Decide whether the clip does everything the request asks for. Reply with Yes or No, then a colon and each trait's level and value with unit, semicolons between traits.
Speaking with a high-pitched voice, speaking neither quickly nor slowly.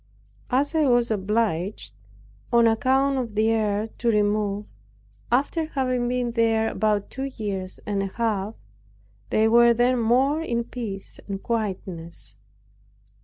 No: high, 225 Hz; slow, 130 wpm